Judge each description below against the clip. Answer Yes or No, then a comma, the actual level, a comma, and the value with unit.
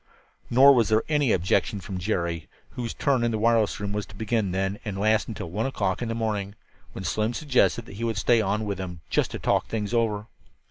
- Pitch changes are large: No, average, 2.9 semitones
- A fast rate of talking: Yes, fast, 225 wpm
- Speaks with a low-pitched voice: Yes, low, 110 Hz